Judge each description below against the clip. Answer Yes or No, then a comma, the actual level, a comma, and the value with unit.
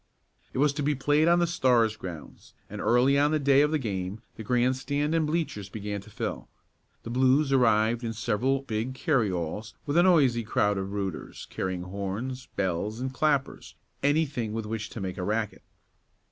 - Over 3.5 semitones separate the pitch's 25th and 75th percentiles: Yes, average, 5.2 semitones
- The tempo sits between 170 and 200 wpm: Yes, average, 180 wpm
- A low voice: Yes, low, 120 Hz